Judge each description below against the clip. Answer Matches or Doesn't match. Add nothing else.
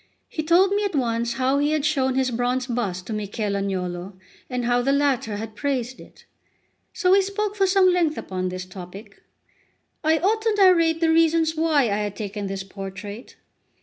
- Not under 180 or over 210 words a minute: Matches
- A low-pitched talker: Doesn't match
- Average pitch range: Doesn't match